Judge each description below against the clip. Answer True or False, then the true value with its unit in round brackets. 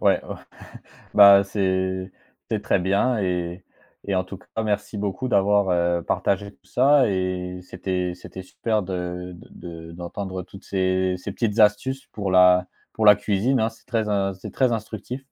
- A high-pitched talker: False (95 Hz)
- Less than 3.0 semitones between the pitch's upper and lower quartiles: True (2.4 semitones)